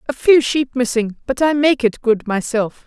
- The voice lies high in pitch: Yes, very high, 250 Hz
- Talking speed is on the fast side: Yes, fast, 210 wpm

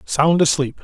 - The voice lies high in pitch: No, medium, 150 Hz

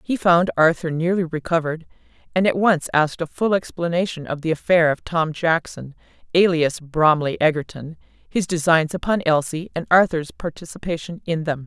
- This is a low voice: No, medium, 165 Hz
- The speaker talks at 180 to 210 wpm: No, average, 155 wpm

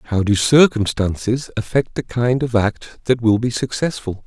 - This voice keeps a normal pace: Yes, average, 170 wpm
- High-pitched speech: No, low, 115 Hz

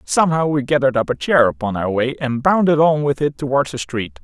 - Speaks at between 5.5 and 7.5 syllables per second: Yes, 5.8 syllables/s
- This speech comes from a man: Yes, male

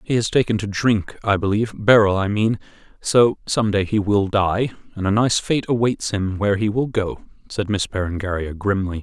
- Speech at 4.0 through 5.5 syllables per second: Yes, 5.2 syllables/s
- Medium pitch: No, low, 105 Hz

